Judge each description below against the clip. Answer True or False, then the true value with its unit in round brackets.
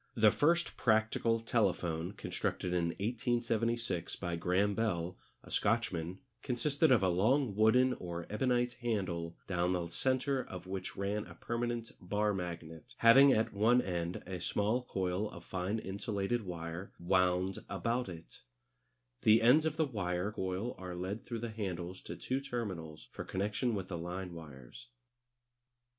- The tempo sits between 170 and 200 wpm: False (150 wpm)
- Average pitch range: True (4.7 semitones)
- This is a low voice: True (100 Hz)